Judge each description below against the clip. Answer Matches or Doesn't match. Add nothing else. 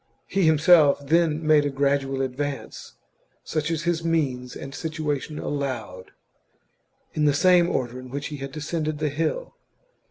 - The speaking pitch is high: Doesn't match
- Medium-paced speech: Matches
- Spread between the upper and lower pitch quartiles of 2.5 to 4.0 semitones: Matches